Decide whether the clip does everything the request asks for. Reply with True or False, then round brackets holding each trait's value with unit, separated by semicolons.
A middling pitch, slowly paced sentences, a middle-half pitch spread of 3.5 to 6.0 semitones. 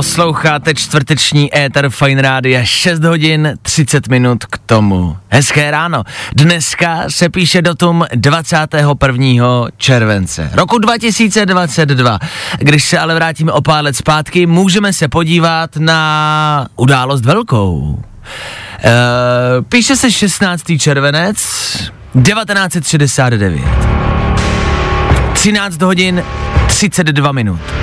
True (150 Hz; 95 wpm; 5.6 semitones)